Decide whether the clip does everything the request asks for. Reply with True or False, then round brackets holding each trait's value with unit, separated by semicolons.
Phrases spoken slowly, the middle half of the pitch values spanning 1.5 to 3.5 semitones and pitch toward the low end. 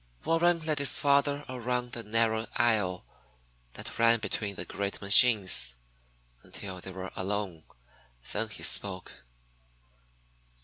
False (120 wpm; 4.1 semitones; 110 Hz)